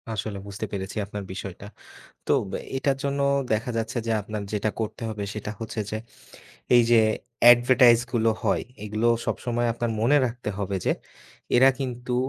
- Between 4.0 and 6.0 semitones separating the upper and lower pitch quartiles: No, narrow, 2.4 semitones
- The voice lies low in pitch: Yes, low, 115 Hz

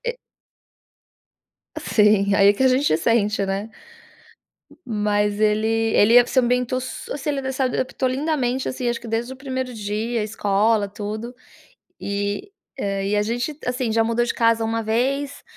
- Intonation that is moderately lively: Yes, average, 3.5 semitones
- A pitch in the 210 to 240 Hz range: Yes, high, 230 Hz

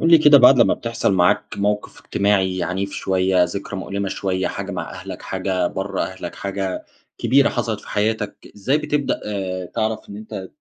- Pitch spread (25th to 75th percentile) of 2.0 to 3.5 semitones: Yes, average, 2.7 semitones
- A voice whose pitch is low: Yes, low, 100 Hz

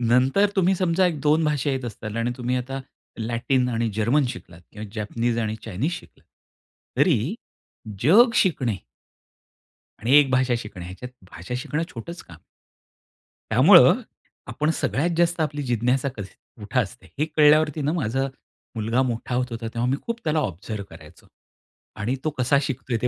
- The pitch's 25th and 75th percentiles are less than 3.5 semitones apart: No, average, 4.7 semitones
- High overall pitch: No, low, 125 Hz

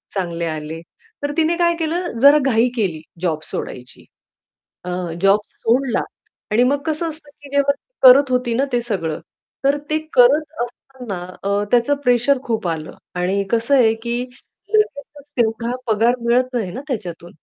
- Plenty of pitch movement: Yes, wide, 6.1 semitones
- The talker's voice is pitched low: No, high, 240 Hz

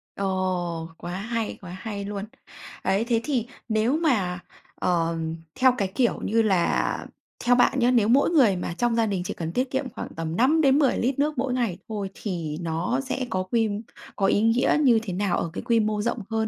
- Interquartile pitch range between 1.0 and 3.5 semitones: No, average, 5.0 semitones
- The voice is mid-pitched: No, high, 220 Hz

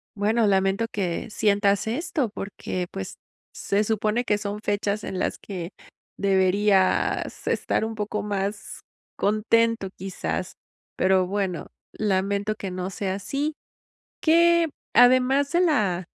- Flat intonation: No, average, 3.0 semitones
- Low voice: No, high, 205 Hz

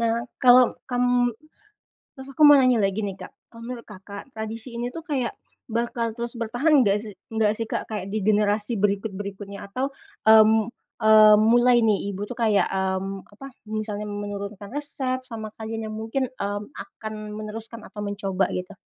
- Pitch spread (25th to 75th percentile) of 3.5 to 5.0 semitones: No, average, 2.9 semitones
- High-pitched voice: Yes, high, 220 Hz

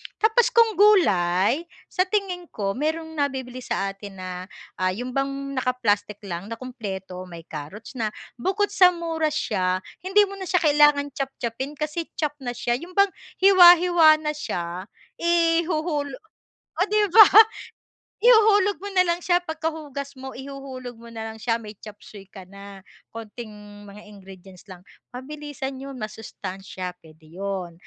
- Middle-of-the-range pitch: No, very high, 265 Hz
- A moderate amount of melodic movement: No, wide, 8.7 semitones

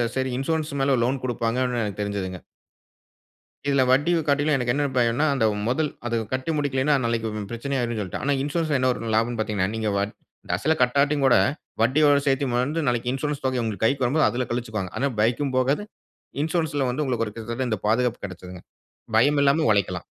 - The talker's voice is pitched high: No, low, 125 Hz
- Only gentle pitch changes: No, average, 3.8 semitones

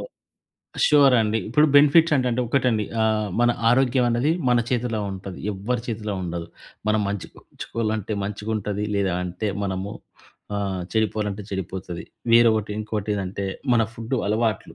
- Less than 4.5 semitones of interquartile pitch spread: Yes, average, 3.2 semitones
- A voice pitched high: No, low, 110 Hz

